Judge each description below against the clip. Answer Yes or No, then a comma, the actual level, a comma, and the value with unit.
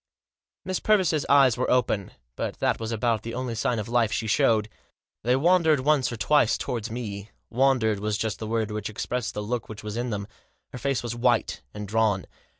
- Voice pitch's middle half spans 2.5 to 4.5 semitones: Yes, average, 2.8 semitones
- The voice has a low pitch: Yes, low, 115 Hz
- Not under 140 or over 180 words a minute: No, average, 200 wpm